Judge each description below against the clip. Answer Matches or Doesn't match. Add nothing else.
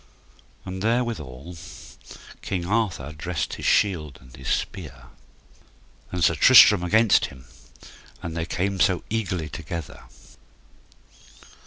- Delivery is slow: Matches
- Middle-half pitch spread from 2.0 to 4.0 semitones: Doesn't match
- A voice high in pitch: Doesn't match